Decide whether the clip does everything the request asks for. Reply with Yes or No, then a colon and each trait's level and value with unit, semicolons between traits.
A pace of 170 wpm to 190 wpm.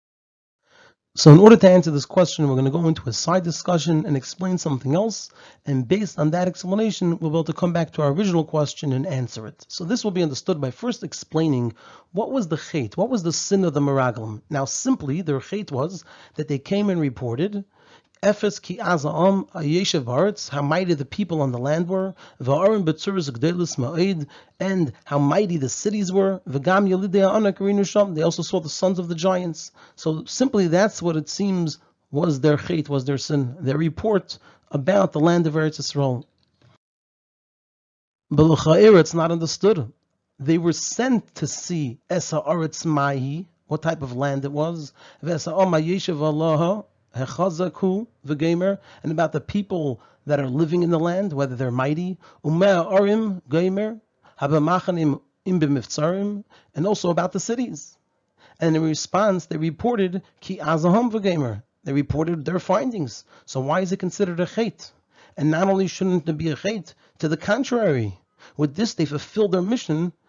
No: average, 155 wpm